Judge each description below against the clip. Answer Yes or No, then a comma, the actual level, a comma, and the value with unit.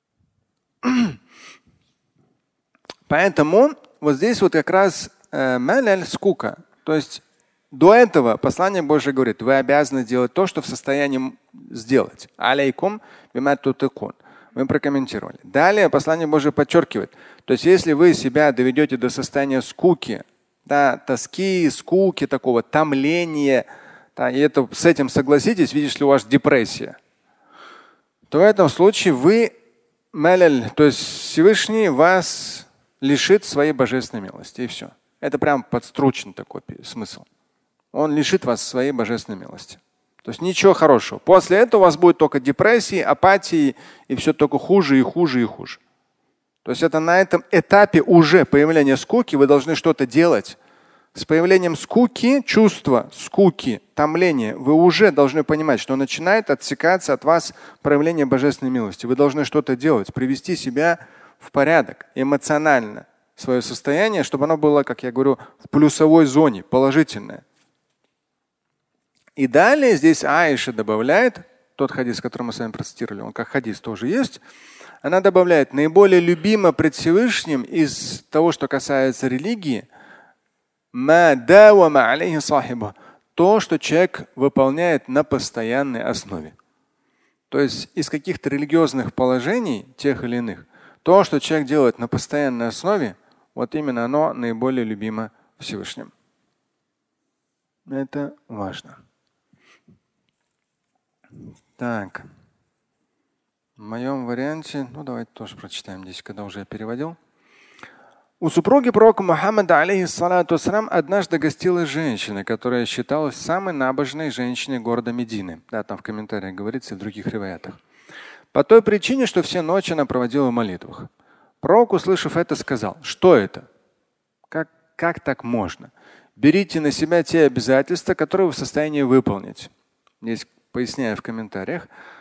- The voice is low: No, medium, 150 Hz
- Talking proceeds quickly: No, average, 130 wpm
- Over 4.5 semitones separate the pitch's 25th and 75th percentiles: Yes, average, 5.3 semitones